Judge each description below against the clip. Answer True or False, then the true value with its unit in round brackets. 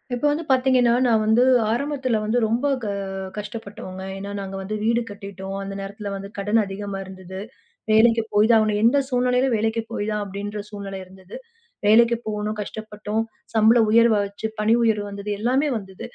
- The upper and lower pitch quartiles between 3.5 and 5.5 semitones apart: False (2.6 semitones)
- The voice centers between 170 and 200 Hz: False (215 Hz)